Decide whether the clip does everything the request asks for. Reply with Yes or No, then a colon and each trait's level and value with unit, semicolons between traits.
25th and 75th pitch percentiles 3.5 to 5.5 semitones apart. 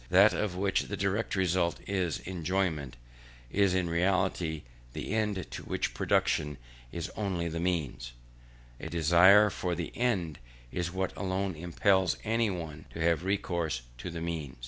No: average, 2.8 semitones